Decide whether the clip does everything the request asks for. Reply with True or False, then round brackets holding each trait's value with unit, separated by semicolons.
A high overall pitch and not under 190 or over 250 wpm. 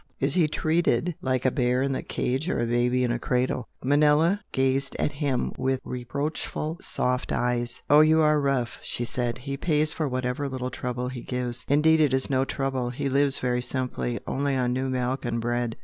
False (130 Hz; 195 wpm)